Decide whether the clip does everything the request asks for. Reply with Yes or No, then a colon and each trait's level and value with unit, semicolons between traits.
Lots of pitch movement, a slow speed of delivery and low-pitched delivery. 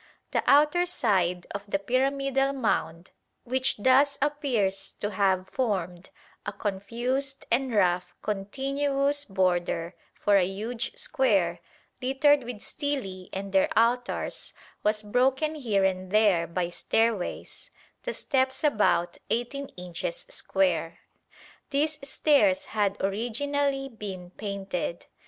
No: wide, 6.2 semitones; slow, 115 wpm; high, 225 Hz